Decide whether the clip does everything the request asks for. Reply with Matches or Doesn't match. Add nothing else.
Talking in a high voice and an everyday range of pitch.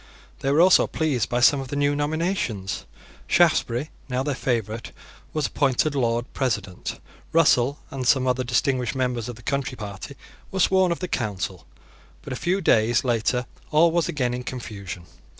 Doesn't match